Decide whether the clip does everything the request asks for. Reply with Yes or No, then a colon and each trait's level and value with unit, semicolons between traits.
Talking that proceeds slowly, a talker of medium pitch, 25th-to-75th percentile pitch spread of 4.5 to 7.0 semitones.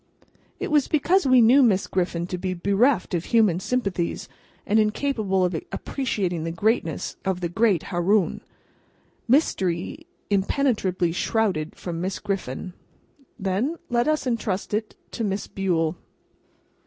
No: slow, 130 wpm; high, 195 Hz; average, 4.9 semitones